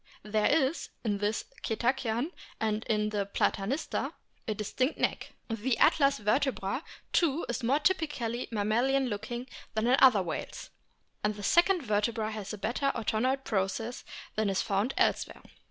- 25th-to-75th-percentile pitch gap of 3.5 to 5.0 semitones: Yes, average, 4.1 semitones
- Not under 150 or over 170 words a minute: No, average, 140 wpm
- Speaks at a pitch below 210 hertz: No, high, 225 Hz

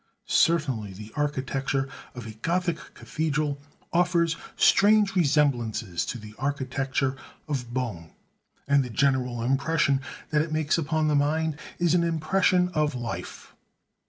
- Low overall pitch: No, medium, 145 Hz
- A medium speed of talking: No, slow, 130 wpm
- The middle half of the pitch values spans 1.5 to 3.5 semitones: No, average, 4.0 semitones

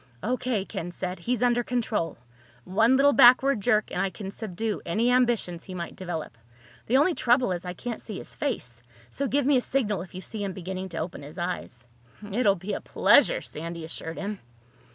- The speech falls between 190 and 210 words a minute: Yes, average, 200 wpm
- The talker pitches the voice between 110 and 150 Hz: No, high, 205 Hz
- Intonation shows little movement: No, wide, 5.6 semitones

